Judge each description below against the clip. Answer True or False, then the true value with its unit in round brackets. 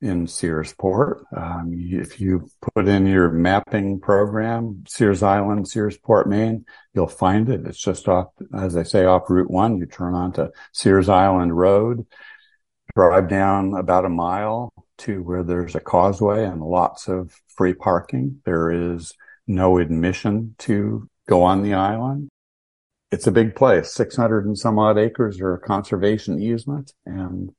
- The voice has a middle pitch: False (95 Hz)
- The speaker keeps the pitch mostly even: False (3.2 semitones)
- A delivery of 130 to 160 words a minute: True (150 wpm)